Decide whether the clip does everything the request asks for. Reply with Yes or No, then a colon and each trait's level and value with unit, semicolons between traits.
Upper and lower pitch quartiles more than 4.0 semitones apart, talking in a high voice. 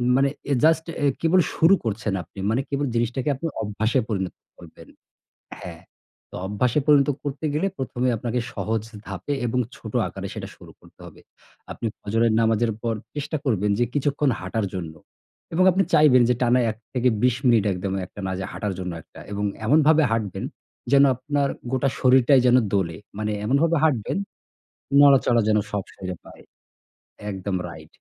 No: average, 5.2 semitones; low, 120 Hz